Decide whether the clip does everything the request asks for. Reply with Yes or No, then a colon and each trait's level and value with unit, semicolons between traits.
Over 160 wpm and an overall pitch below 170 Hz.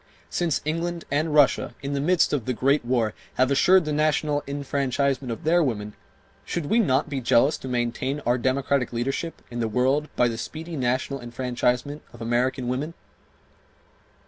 Yes: average, 170 wpm; low, 135 Hz